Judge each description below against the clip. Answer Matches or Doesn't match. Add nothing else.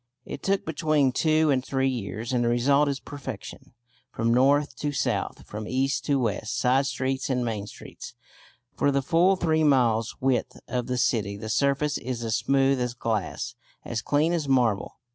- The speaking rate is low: Doesn't match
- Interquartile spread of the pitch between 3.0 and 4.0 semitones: Matches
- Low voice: Matches